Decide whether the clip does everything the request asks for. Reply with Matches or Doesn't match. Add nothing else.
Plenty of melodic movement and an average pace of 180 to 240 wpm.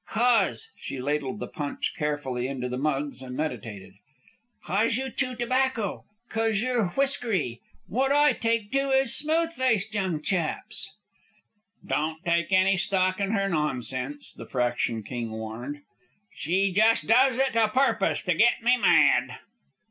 Doesn't match